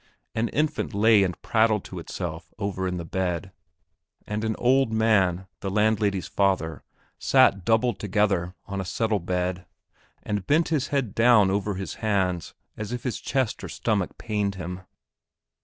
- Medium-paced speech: Yes, average, 155 wpm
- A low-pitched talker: Yes, low, 100 Hz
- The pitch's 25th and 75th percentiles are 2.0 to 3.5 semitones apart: Yes, average, 3.2 semitones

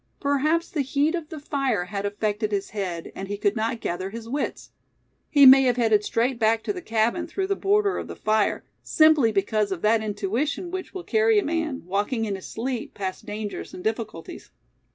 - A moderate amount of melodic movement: No, wide, 6.5 semitones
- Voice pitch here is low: No, high, 230 Hz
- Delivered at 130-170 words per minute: No, average, 200 wpm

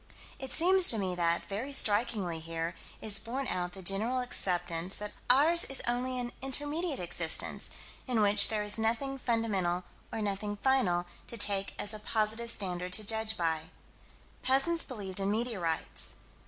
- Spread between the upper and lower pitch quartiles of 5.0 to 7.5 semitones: Yes, average, 5.3 semitones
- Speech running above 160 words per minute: No, average, 155 wpm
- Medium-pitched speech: No, high, 215 Hz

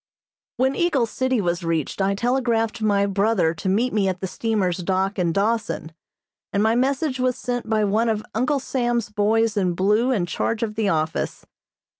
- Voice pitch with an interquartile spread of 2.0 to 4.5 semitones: Yes, average, 3.8 semitones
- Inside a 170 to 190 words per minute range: Yes, average, 180 wpm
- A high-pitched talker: Yes, high, 215 Hz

